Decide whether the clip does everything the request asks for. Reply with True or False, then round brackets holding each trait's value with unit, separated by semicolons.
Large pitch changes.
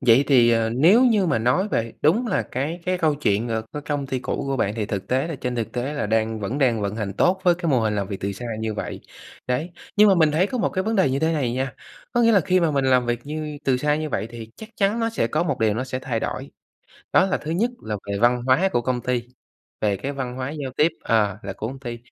True (5.9 semitones)